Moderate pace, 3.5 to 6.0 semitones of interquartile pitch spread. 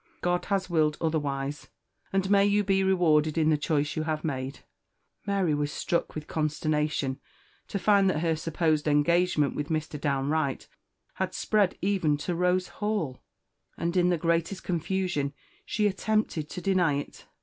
Yes: average, 160 wpm; average, 3.8 semitones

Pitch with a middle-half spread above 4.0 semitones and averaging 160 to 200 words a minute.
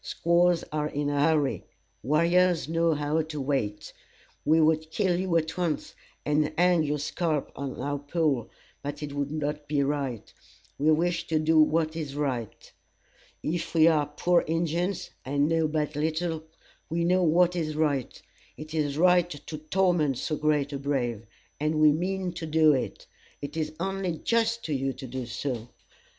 No: average, 2.7 semitones; average, 170 wpm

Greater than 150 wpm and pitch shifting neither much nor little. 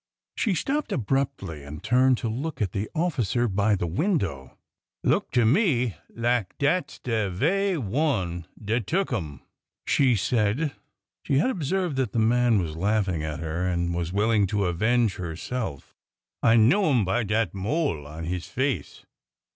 No: average, 160 wpm; wide, 6.7 semitones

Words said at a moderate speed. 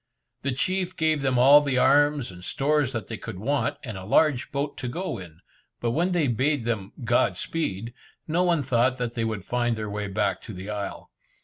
No: fast, 210 wpm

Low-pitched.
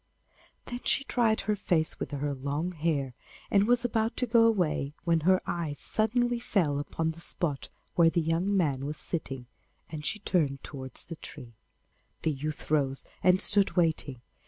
No: medium, 165 Hz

